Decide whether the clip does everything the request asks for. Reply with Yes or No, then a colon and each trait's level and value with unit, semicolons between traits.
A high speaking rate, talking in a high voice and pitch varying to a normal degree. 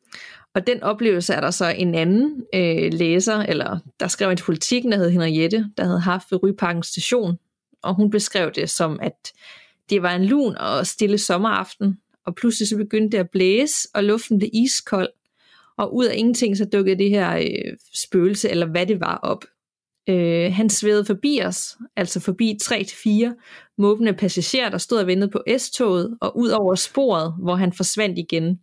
No: average, 180 wpm; high, 200 Hz; average, 3.5 semitones